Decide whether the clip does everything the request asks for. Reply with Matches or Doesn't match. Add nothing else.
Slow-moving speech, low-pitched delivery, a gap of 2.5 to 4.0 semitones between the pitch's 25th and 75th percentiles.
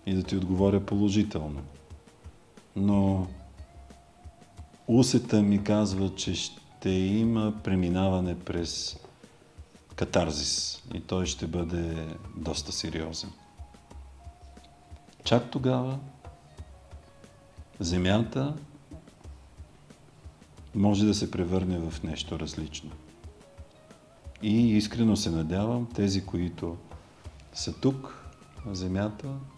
Doesn't match